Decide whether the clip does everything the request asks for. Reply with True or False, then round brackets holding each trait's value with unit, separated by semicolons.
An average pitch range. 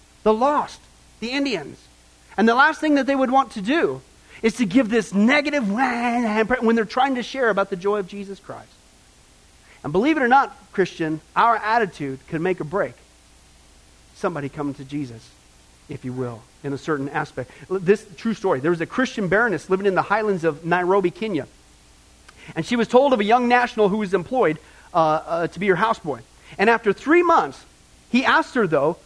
False (8.2 semitones)